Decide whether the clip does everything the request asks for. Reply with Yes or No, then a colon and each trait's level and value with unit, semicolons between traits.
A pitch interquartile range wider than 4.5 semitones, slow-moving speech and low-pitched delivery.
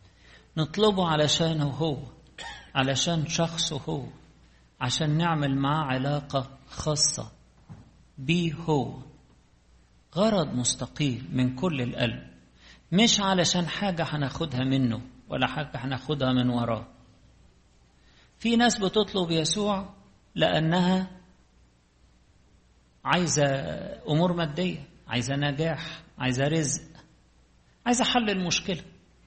No: average, 5.2 semitones; slow, 90 wpm; medium, 150 Hz